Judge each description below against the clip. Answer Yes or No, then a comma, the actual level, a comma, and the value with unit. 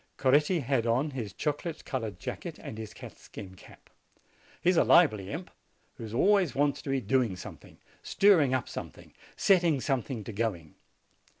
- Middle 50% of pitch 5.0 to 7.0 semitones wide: Yes, wide, 5.6 semitones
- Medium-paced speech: Yes, average, 170 wpm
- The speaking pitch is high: No, low, 130 Hz